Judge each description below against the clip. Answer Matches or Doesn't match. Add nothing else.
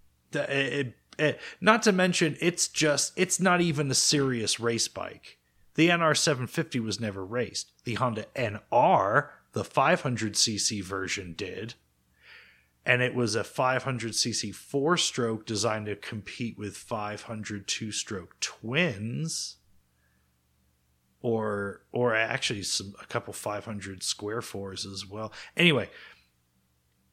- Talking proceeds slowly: Matches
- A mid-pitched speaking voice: Doesn't match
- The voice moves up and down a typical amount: Doesn't match